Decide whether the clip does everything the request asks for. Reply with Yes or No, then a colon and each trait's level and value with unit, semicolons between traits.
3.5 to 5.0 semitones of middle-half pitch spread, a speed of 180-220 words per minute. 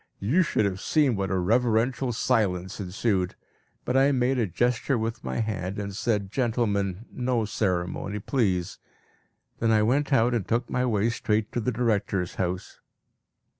No: average, 3.9 semitones; average, 160 wpm